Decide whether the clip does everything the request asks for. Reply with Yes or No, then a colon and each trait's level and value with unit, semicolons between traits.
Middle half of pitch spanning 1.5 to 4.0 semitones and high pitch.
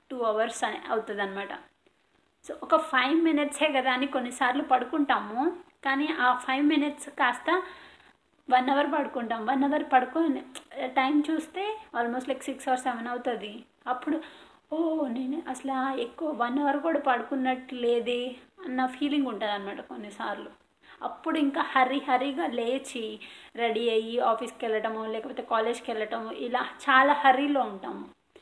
Yes: average, 3.5 semitones; very high, 260 Hz